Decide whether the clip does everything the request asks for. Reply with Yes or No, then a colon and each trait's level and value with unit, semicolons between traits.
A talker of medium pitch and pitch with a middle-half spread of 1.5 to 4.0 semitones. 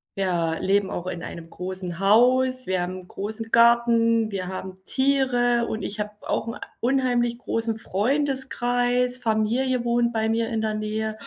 No: high, 225 Hz; average, 3.7 semitones